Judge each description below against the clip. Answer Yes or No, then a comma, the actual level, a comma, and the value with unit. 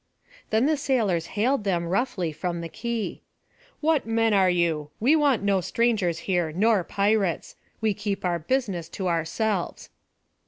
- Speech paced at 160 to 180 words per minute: No, average, 150 wpm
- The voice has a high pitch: Yes, high, 200 Hz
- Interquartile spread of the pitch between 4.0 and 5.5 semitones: Yes, average, 4.8 semitones